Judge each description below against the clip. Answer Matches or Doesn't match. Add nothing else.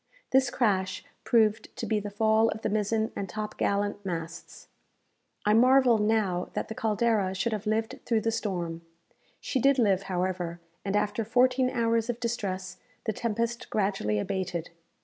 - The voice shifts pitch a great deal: Doesn't match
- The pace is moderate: Matches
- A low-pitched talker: Doesn't match